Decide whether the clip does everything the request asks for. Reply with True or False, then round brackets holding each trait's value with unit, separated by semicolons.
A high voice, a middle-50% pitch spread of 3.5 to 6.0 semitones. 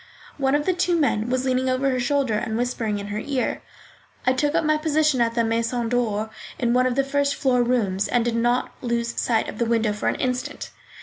False (245 Hz; 2.9 semitones)